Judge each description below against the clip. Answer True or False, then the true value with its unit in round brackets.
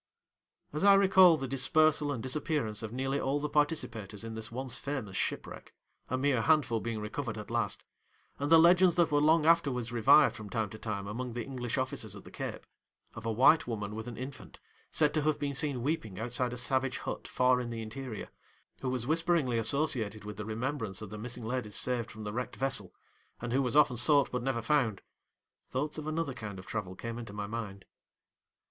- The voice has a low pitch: True (125 Hz)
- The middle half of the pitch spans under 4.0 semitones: False (4.6 semitones)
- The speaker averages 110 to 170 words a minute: False (205 wpm)